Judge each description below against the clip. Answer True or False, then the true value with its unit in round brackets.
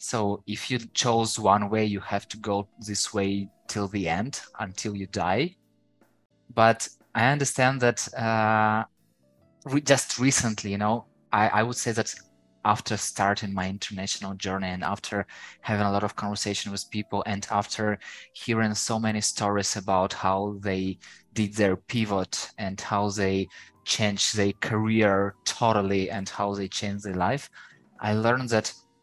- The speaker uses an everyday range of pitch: False (2.0 semitones)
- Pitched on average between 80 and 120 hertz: True (105 Hz)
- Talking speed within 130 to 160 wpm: True (155 wpm)